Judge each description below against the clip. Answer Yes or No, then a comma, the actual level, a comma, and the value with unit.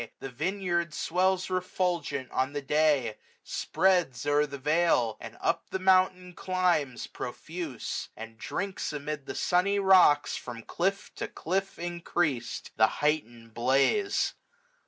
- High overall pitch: No, medium, 155 Hz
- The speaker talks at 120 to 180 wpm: Yes, slow, 135 wpm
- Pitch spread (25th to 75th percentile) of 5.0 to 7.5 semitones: Yes, wide, 5.4 semitones